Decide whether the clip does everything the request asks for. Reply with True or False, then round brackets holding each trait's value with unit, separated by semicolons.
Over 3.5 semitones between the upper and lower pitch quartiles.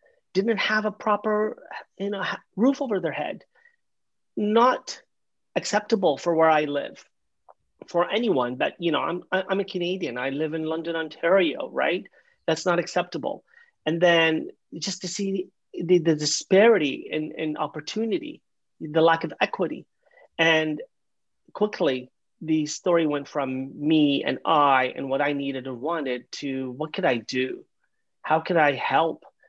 True (4.5 semitones)